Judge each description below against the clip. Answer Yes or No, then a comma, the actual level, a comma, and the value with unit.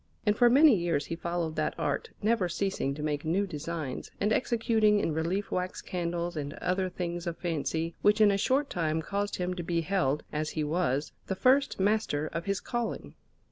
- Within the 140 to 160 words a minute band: No, average, 195 wpm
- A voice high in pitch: No, medium, 175 Hz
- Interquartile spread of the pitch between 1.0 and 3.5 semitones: No, average, 4.2 semitones